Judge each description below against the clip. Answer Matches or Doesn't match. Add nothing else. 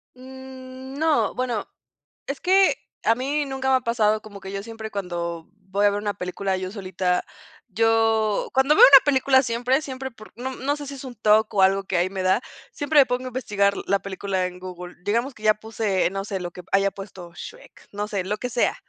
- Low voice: Doesn't match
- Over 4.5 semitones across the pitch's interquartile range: Matches